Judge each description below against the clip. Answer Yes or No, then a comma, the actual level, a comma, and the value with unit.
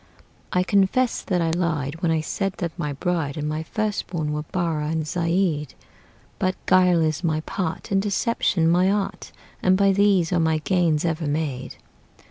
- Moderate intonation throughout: Yes, average, 3.2 semitones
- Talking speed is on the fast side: No, average, 175 wpm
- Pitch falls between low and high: Yes, medium, 170 Hz